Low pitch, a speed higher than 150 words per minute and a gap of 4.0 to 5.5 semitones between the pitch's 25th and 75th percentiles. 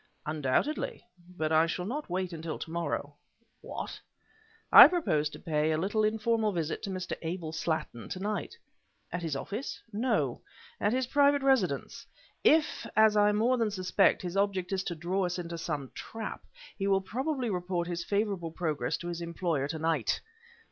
No: medium, 185 Hz; average, 170 wpm; average, 4.6 semitones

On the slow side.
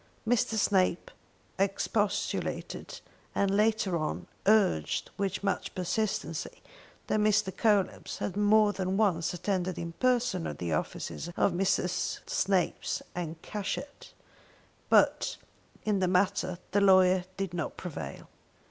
Yes: slow, 120 wpm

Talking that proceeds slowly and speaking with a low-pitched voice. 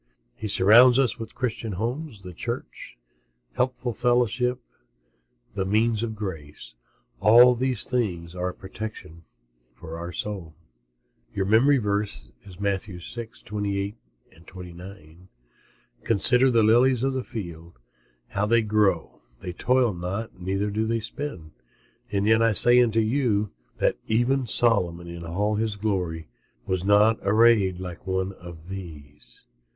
Yes: slow, 130 wpm; low, 105 Hz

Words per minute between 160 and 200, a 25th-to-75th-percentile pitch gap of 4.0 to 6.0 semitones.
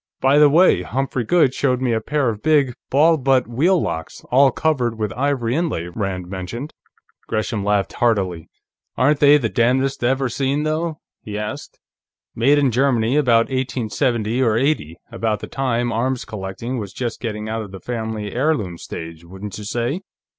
Yes: average, 170 wpm; average, 4.3 semitones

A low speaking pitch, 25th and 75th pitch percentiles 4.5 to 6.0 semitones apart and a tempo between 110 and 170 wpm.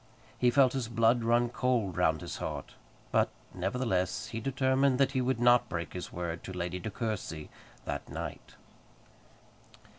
Yes: low, 115 Hz; wide, 5.6 semitones; average, 155 wpm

